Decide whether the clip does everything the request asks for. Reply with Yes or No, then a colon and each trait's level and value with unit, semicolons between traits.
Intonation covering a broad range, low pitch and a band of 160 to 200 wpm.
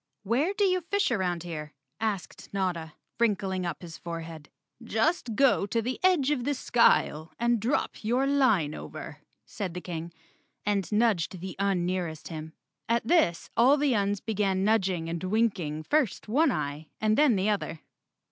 No: wide, 5.7 semitones; high, 200 Hz; average, 165 wpm